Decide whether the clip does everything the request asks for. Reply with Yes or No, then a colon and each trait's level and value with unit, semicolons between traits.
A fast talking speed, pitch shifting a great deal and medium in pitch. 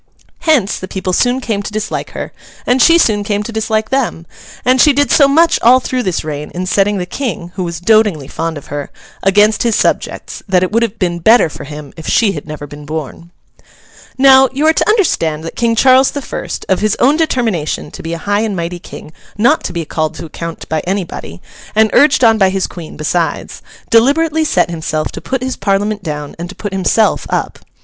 No: fast, 210 wpm; wide, 6.6 semitones; high, 205 Hz